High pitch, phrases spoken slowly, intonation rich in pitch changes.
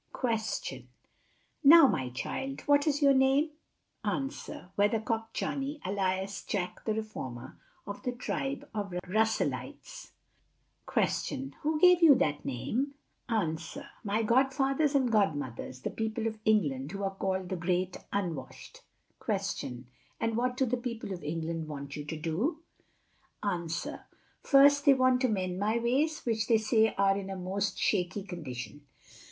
No: high, 215 Hz; average, 145 wpm; wide, 6.6 semitones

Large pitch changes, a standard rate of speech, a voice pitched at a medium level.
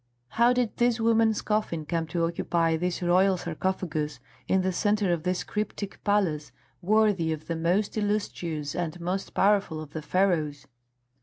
No: average, 4.1 semitones; average, 155 wpm; medium, 180 Hz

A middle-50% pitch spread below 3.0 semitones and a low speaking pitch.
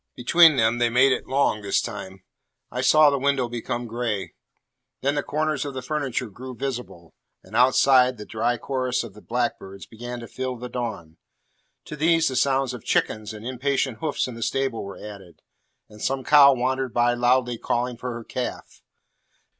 Yes: narrow, 2.6 semitones; low, 125 Hz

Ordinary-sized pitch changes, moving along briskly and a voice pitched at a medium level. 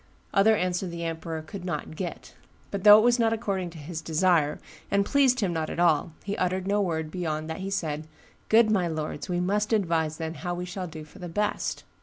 Yes: average, 3.7 semitones; fast, 220 wpm; medium, 180 Hz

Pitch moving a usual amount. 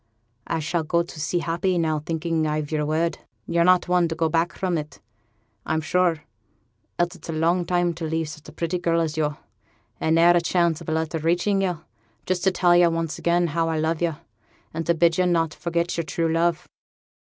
No: narrow, 1.4 semitones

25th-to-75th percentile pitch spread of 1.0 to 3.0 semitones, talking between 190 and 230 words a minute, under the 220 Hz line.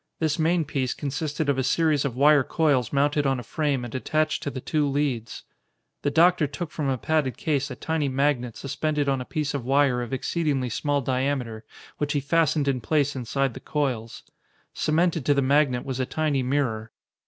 Yes: average, 2.7 semitones; average, 195 wpm; medium, 140 Hz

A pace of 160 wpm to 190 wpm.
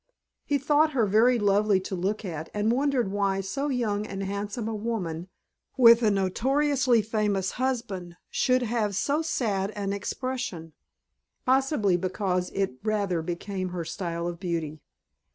No: average, 145 wpm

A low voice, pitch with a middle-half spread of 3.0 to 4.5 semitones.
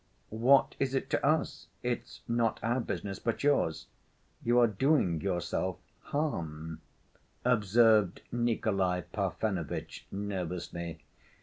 No: low, 110 Hz; average, 5.3 semitones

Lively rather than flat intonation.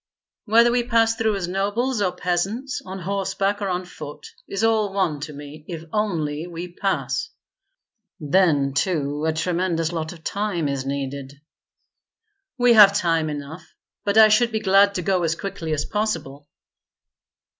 No: average, 4.8 semitones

